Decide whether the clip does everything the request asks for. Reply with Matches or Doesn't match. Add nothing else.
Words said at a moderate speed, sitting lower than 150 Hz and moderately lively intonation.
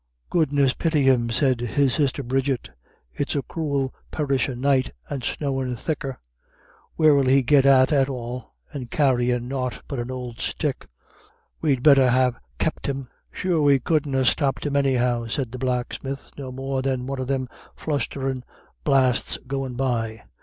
Doesn't match